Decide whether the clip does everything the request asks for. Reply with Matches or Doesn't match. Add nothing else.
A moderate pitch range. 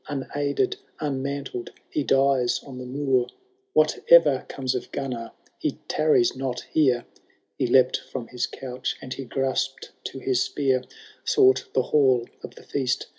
Doesn't match